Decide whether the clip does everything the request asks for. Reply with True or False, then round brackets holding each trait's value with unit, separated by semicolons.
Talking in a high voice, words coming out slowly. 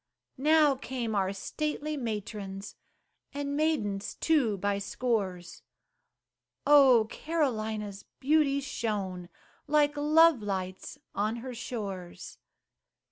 True (230 Hz; 90 wpm)